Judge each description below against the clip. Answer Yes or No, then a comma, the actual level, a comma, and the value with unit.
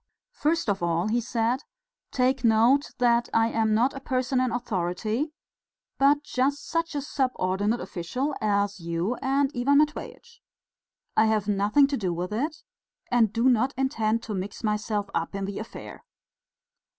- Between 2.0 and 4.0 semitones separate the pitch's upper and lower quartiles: No, average, 4.6 semitones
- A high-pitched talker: Yes, high, 230 Hz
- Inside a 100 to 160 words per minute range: Yes, average, 155 wpm